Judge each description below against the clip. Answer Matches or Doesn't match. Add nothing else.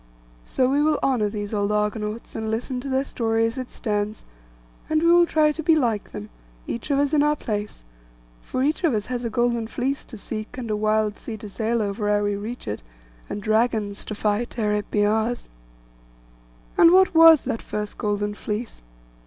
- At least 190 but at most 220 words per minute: Matches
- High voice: Matches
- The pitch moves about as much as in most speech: Matches